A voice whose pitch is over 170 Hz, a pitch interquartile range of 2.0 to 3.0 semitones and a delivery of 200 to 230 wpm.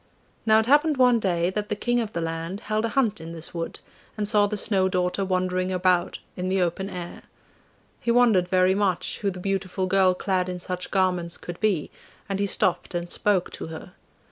Yes: medium, 185 Hz; narrow, 2.6 semitones; fast, 205 wpm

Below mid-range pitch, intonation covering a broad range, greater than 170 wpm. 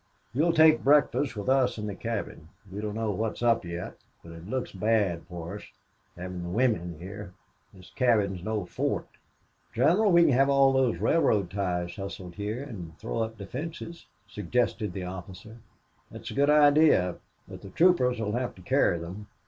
Yes: low, 105 Hz; wide, 6.0 semitones; average, 180 wpm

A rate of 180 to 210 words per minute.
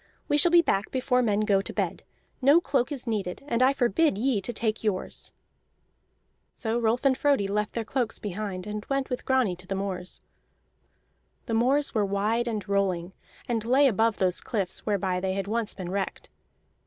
Yes: average, 185 wpm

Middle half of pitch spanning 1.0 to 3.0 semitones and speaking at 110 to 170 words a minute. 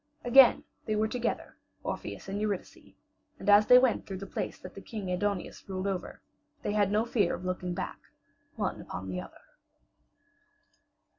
Yes: average, 2.7 semitones; average, 160 wpm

